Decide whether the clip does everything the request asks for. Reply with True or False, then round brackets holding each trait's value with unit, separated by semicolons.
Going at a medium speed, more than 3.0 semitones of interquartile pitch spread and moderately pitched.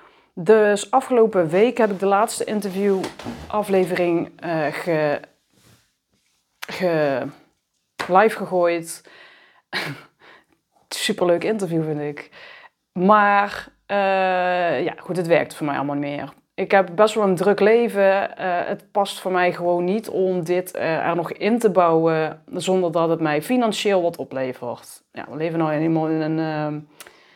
True (145 wpm; 3.8 semitones; 180 Hz)